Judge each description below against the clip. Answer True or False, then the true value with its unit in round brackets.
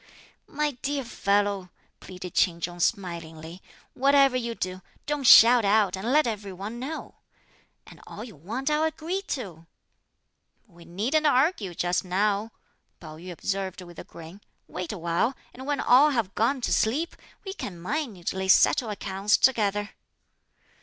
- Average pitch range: False (6.4 semitones)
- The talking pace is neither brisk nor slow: True (150 wpm)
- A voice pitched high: True (205 Hz)